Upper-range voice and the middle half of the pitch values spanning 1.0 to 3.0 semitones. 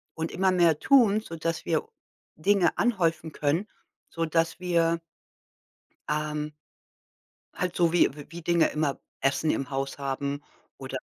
No: medium, 165 Hz; average, 2.7 semitones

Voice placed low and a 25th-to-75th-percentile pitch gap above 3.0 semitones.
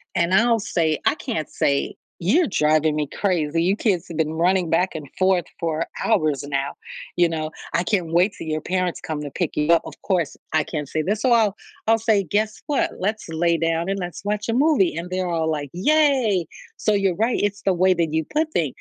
No: medium, 175 Hz; average, 4.4 semitones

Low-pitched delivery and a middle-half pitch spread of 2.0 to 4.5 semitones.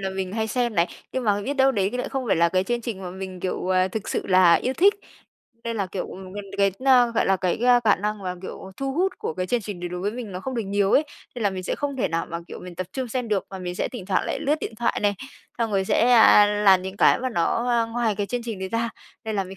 No: high, 205 Hz; average, 4.2 semitones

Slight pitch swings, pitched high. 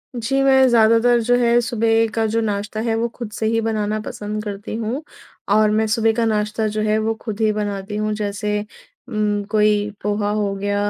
Yes: narrow, 1.4 semitones; high, 215 Hz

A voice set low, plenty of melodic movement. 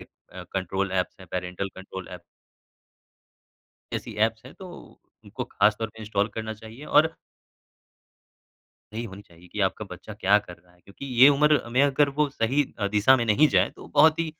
Yes: low, 110 Hz; wide, 6.3 semitones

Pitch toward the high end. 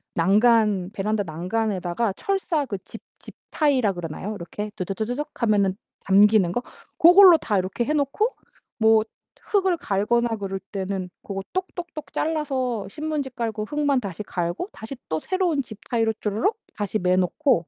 Yes: high, 220 Hz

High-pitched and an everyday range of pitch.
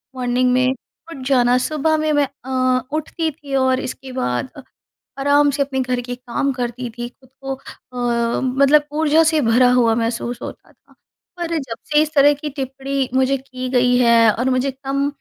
No: very high, 265 Hz; narrow, 2.2 semitones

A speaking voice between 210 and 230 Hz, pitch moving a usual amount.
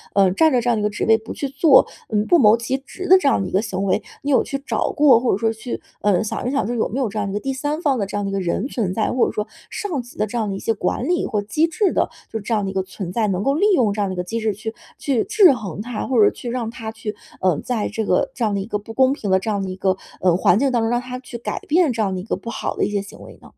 Yes: high, 225 Hz; average, 4.3 semitones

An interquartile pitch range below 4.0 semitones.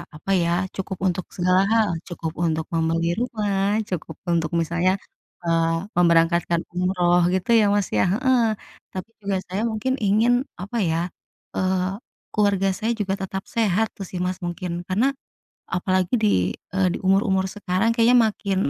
Yes: average, 2.9 semitones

